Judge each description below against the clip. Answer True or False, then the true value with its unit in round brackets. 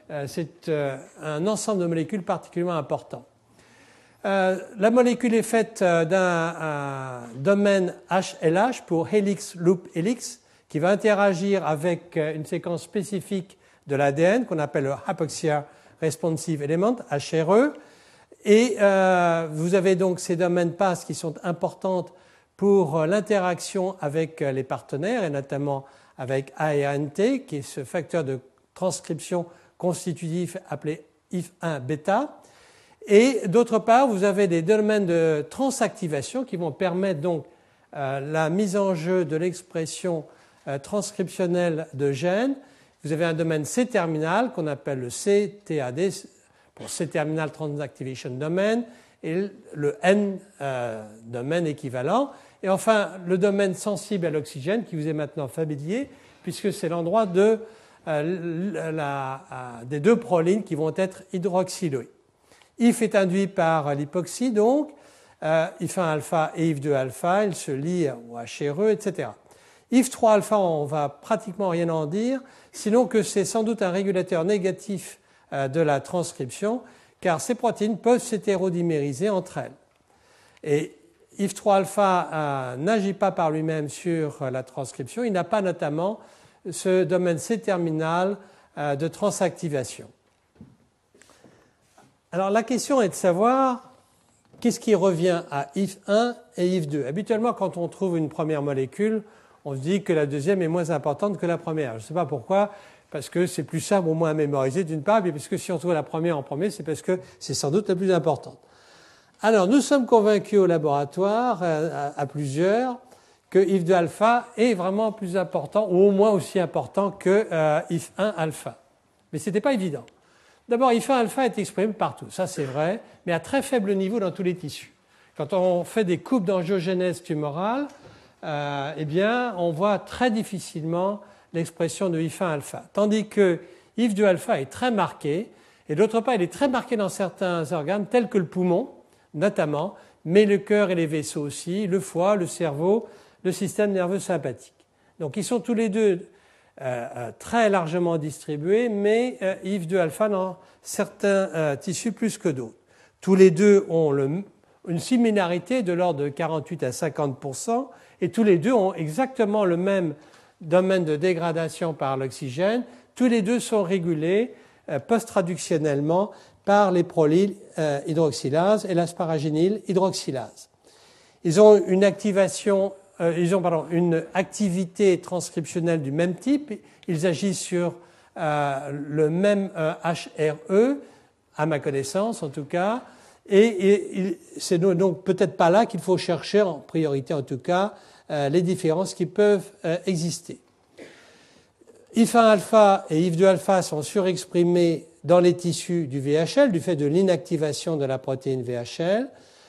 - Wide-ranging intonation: False (4.3 semitones)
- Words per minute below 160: True (150 wpm)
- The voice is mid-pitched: True (180 Hz)